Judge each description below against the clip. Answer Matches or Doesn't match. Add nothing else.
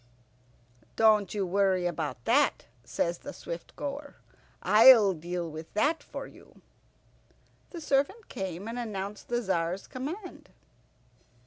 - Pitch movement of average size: Doesn't match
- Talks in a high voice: Matches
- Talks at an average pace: Doesn't match